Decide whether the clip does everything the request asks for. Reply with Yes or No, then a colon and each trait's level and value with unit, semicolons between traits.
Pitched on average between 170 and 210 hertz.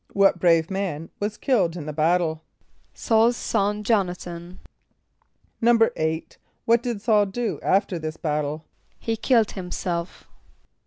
Yes: medium, 185 Hz